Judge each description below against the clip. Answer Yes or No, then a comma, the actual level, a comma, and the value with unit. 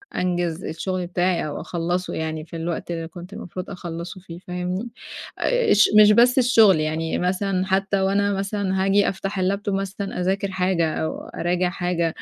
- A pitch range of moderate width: No, narrow, 2.3 semitones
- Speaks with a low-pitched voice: No, medium, 185 Hz